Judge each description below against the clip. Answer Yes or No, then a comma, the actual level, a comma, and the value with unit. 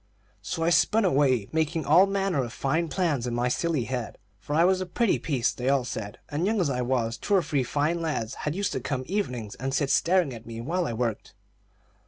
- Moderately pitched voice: Yes, medium, 145 Hz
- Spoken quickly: Yes, fast, 225 wpm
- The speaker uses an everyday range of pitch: No, wide, 5.8 semitones